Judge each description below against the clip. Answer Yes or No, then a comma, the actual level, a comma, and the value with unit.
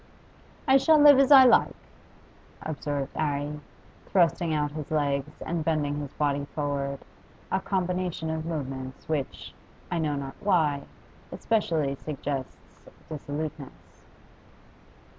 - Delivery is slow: Yes, slow, 115 wpm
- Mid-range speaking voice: Yes, medium, 150 Hz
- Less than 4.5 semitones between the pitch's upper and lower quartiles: Yes, average, 3.2 semitones